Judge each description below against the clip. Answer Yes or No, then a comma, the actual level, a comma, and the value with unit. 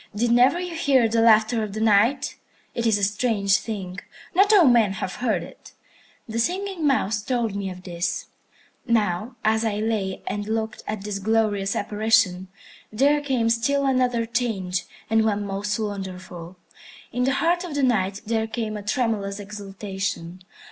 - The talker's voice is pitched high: Yes, high, 220 Hz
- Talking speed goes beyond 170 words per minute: No, average, 165 wpm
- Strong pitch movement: No, average, 3.5 semitones